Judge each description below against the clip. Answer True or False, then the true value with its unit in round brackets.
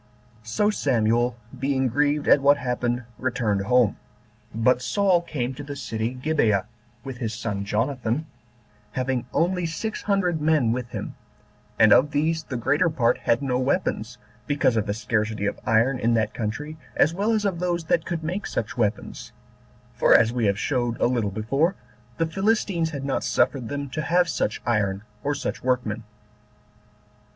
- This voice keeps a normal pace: True (165 wpm)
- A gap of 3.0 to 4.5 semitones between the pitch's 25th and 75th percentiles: False (5.6 semitones)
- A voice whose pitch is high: False (130 Hz)